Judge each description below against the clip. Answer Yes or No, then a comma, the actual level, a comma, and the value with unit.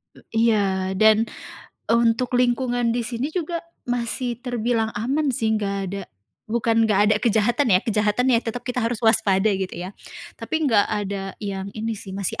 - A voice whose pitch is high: Yes, high, 225 Hz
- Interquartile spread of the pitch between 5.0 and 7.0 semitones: No, average, 2.9 semitones